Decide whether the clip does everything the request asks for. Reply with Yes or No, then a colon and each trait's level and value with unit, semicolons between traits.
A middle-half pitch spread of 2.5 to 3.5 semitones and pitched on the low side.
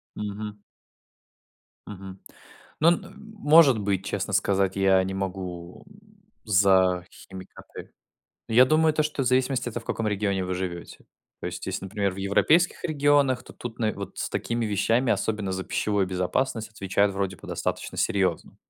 No: average, 4.8 semitones; low, 100 Hz